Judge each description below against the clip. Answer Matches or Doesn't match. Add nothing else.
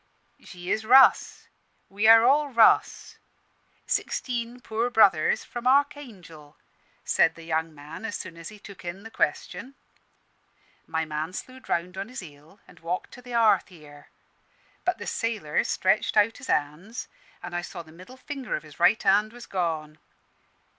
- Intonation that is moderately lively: Doesn't match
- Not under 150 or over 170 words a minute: Matches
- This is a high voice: Matches